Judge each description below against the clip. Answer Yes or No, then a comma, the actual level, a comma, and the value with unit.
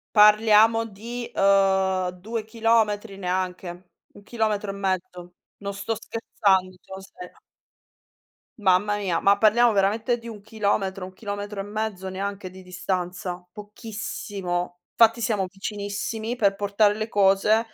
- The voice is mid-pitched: No, high, 200 Hz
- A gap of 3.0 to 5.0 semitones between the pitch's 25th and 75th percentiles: No, narrow, 2.4 semitones